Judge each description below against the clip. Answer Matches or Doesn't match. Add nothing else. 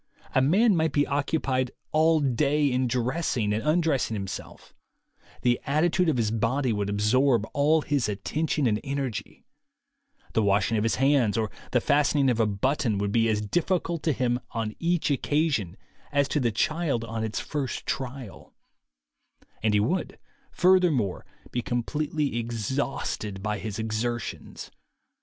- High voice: Doesn't match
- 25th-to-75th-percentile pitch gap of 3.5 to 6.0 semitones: Matches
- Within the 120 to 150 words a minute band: Matches